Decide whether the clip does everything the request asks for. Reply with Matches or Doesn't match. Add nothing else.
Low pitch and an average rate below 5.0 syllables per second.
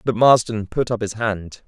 Matches